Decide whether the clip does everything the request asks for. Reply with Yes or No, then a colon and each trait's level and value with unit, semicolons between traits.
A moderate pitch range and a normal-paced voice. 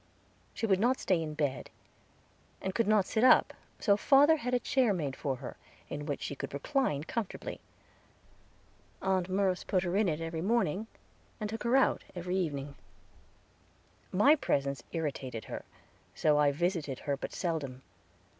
No: wide, 6.7 semitones; average, 160 wpm